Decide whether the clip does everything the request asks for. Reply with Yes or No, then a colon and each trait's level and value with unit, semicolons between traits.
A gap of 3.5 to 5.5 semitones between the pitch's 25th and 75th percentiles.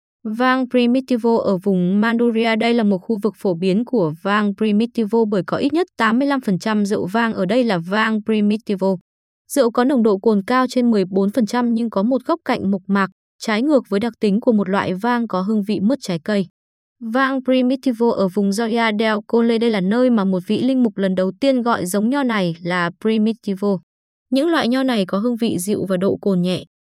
Yes: average, 3.8 semitones